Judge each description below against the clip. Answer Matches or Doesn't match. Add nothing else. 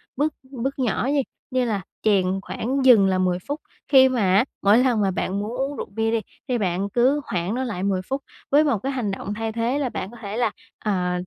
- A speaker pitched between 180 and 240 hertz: Matches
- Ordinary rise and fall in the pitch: Matches